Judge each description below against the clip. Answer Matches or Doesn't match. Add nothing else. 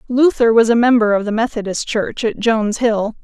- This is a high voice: Matches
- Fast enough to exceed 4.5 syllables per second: Matches